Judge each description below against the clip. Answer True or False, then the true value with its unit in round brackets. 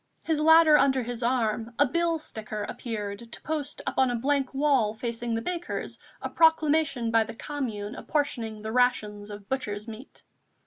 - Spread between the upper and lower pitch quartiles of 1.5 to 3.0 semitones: False (4.8 semitones)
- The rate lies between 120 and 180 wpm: True (165 wpm)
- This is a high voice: True (245 Hz)